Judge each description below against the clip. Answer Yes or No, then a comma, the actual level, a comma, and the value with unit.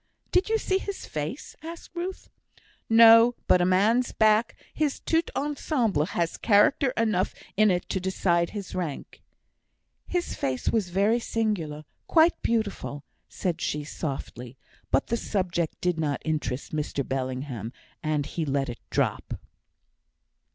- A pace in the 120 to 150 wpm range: Yes, average, 140 wpm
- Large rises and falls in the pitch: Yes, wide, 7.4 semitones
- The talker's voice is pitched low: No, medium, 185 Hz